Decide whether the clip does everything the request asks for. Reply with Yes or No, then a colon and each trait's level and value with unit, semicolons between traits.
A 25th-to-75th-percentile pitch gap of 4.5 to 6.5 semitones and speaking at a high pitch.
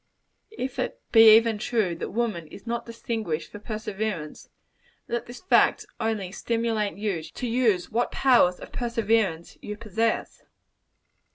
No: average, 2.8 semitones; high, 220 Hz